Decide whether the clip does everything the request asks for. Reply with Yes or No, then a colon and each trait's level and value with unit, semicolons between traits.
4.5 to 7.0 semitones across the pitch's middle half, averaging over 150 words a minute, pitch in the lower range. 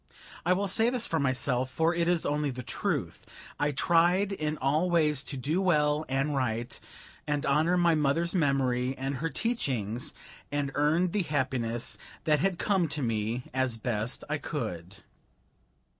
No: average, 4.8 semitones; average, 160 wpm; medium, 145 Hz